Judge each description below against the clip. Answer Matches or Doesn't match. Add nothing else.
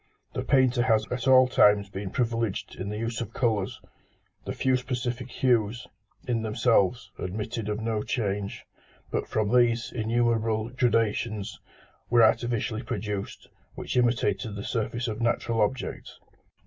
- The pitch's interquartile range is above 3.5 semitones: Doesn't match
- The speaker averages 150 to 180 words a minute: Doesn't match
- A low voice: Matches